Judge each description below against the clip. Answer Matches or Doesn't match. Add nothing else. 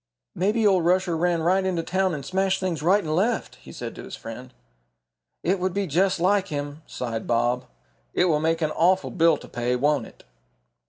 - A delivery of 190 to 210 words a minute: Matches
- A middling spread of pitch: Matches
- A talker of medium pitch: Matches